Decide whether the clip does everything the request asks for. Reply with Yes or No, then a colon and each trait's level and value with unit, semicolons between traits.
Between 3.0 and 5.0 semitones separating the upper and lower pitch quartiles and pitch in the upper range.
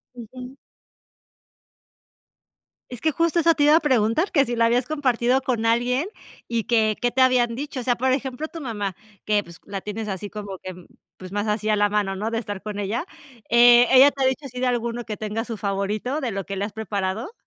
Yes: average, 3.7 semitones; high, 235 Hz